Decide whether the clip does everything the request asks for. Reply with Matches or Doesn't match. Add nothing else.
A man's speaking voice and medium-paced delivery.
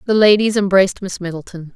Doesn't match